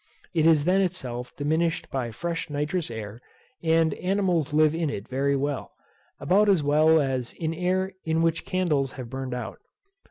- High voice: No, medium, 155 Hz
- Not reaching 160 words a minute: No, average, 165 wpm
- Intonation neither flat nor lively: Yes, average, 4.0 semitones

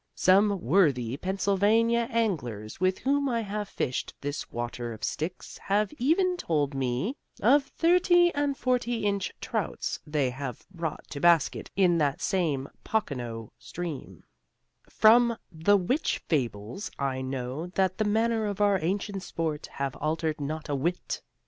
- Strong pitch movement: Yes, wide, 7.8 semitones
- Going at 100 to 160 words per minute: Yes, average, 140 wpm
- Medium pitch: Yes, medium, 180 Hz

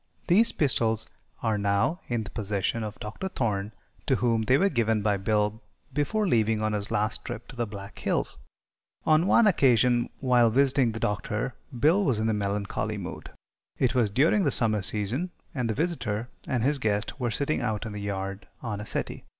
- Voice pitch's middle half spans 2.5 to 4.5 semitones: Yes, average, 4.2 semitones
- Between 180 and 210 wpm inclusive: Yes, average, 190 wpm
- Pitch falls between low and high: No, low, 115 Hz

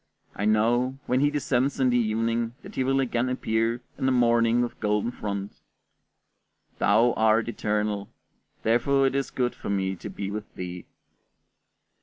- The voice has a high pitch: No, low, 115 Hz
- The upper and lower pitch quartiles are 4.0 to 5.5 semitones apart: No, average, 3.1 semitones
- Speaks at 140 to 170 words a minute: Yes, average, 160 wpm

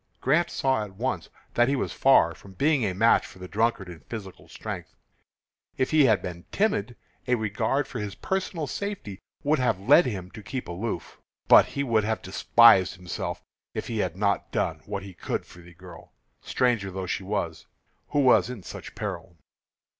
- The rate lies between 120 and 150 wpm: No, average, 185 wpm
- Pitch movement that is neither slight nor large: No, wide, 5.8 semitones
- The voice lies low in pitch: Yes, low, 110 Hz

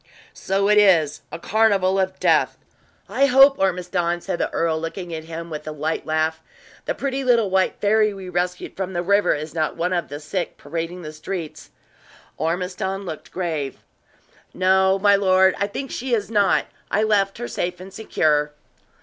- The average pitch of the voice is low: No, medium, 185 Hz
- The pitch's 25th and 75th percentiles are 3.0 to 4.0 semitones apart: Yes, average, 3.5 semitones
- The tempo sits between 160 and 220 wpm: Yes, average, 175 wpm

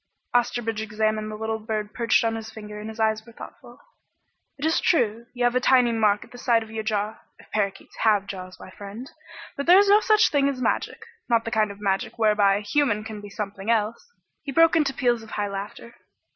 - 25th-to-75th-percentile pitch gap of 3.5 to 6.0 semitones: No, narrow, 2.5 semitones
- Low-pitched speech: No, high, 220 Hz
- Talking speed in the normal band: No, fast, 225 wpm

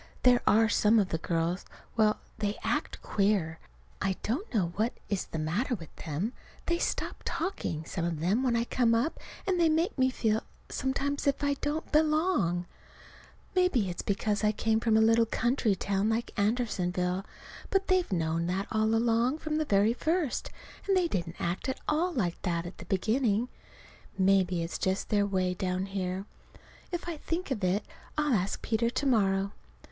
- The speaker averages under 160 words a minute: No, average, 180 wpm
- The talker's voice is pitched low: No, high, 215 Hz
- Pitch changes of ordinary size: No, wide, 6.0 semitones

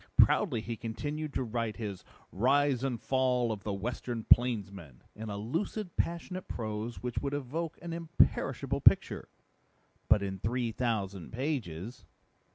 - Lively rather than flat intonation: No, average, 4.9 semitones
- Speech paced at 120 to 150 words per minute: Yes, average, 140 wpm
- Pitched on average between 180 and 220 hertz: No, low, 120 Hz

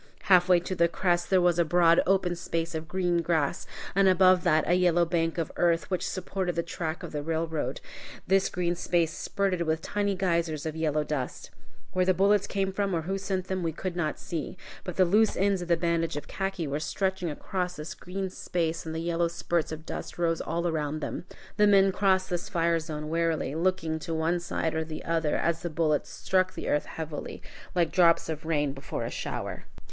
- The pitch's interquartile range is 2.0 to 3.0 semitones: Yes, narrow, 2.4 semitones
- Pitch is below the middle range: No, medium, 170 Hz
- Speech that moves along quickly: Yes, fast, 210 wpm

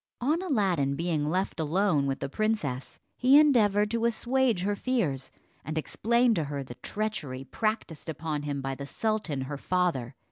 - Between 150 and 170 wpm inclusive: Yes, average, 165 wpm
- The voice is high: No, medium, 180 Hz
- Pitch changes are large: Yes, wide, 7.6 semitones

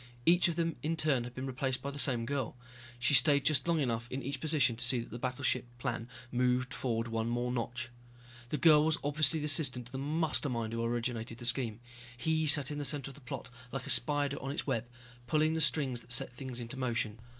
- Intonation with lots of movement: No, average, 3.4 semitones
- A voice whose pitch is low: Yes, low, 130 Hz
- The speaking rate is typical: No, fast, 230 wpm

